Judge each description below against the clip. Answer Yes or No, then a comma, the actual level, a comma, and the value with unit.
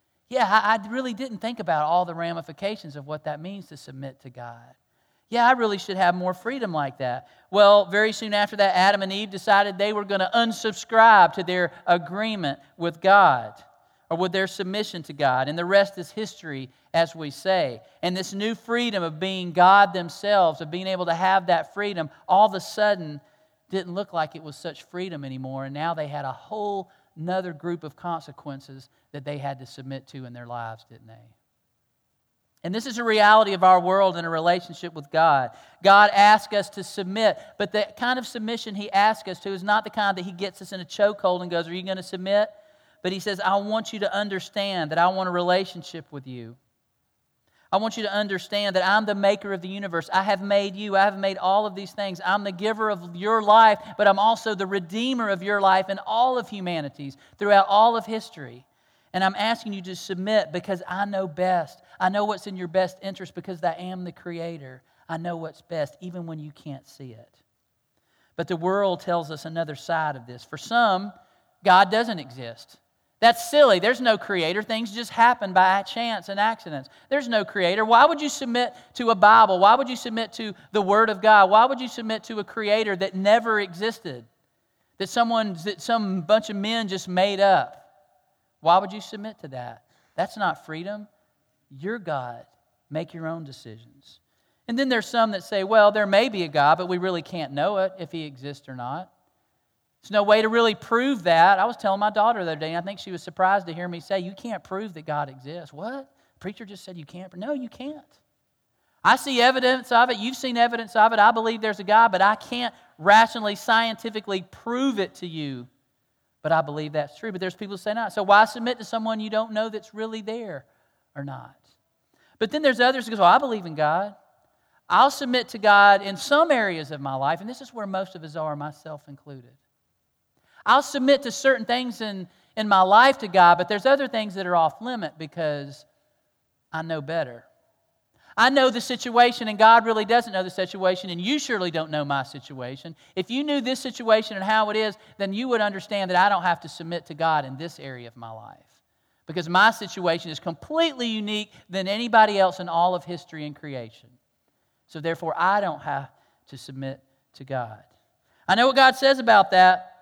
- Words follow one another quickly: Yes, fast, 210 wpm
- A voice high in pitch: Yes, high, 195 Hz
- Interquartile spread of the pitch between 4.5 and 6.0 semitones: Yes, average, 4.9 semitones